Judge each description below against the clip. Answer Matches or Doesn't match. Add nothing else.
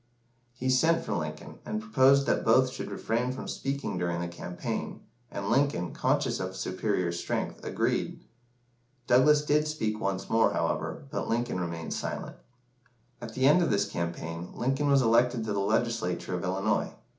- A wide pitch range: Matches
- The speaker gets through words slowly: Doesn't match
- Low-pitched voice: Matches